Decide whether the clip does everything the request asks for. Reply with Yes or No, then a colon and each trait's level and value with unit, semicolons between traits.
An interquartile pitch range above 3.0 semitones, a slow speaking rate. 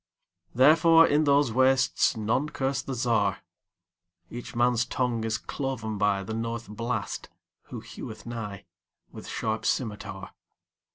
Yes: average, 4.2 semitones; slow, 105 wpm